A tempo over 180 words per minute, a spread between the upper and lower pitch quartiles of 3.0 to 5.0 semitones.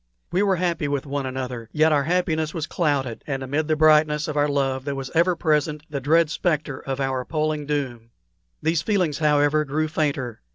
No: average, 195 wpm; narrow, 2.5 semitones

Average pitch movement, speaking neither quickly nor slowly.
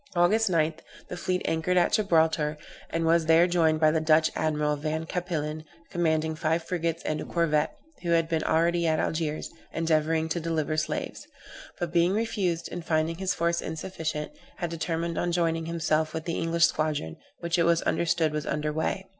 No: narrow, 1.5 semitones; average, 180 wpm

